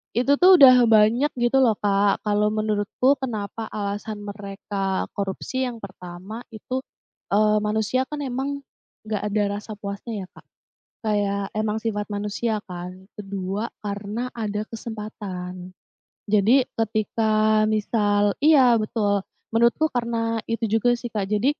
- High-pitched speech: Yes, high, 215 Hz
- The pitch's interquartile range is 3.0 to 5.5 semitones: No, narrow, 2.4 semitones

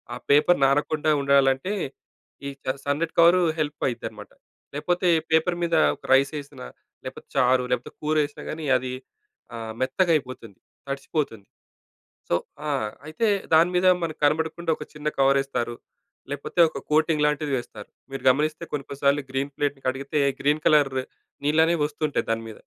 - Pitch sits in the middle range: Yes, medium, 145 Hz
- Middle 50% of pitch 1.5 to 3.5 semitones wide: Yes, average, 2.8 semitones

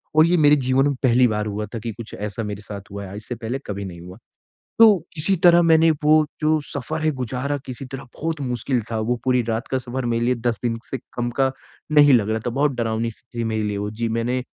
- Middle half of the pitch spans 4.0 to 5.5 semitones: Yes, average, 4.3 semitones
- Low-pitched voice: Yes, low, 120 Hz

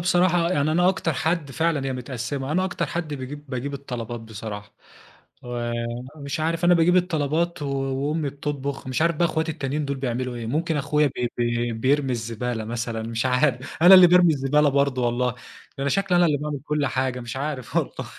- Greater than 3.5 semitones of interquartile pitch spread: Yes, average, 4.2 semitones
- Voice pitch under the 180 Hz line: Yes, medium, 140 Hz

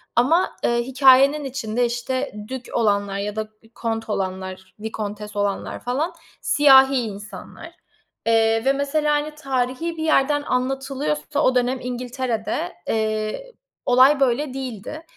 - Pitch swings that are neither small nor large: Yes, average, 3.9 semitones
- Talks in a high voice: Yes, very high, 250 Hz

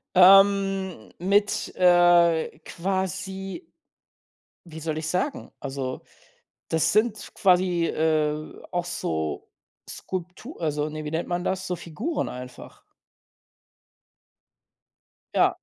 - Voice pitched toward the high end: No, medium, 175 Hz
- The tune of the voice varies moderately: Yes, average, 3.5 semitones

